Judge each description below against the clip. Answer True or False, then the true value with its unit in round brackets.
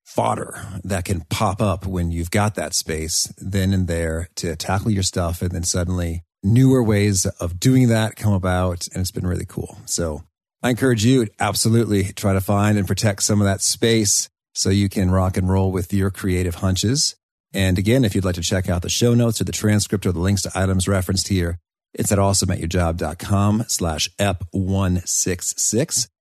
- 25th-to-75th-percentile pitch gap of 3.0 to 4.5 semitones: False (2.4 semitones)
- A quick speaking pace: False (190 wpm)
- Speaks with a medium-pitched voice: False (95 Hz)